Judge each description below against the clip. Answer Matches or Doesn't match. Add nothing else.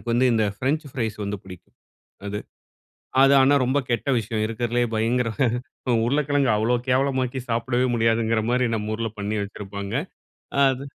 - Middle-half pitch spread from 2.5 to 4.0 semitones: Matches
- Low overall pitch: Matches